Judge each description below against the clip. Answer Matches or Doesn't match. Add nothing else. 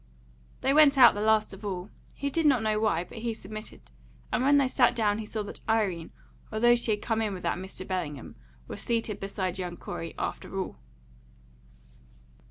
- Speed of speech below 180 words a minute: Doesn't match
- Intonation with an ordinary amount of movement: Matches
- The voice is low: Doesn't match